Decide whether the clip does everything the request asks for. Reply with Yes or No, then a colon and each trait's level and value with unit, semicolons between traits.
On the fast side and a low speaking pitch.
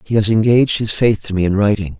Yes: fast, 270 wpm; low, 105 Hz